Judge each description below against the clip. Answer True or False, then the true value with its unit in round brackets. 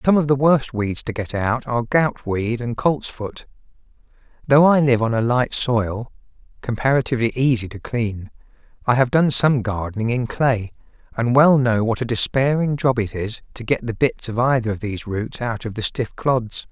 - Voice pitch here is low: True (120 Hz)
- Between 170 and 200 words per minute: True (190 wpm)